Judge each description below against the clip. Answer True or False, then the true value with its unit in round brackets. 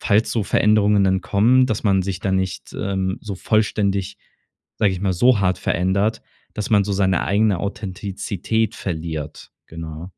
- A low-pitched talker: True (100 Hz)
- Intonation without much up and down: True (2.1 semitones)